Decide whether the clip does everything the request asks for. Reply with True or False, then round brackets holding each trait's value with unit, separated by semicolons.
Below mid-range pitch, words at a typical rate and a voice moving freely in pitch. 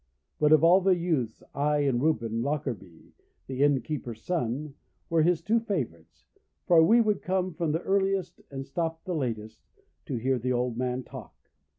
False (150 Hz; 165 wpm; 5.8 semitones)